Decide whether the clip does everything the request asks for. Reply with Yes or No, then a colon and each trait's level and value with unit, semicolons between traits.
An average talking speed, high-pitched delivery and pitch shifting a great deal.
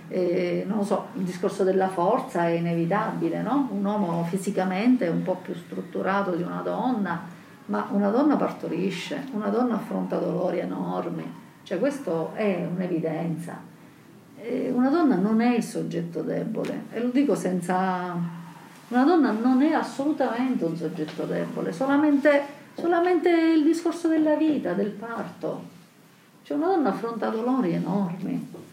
Yes: average, 145 wpm; high, 210 Hz; wide, 6.8 semitones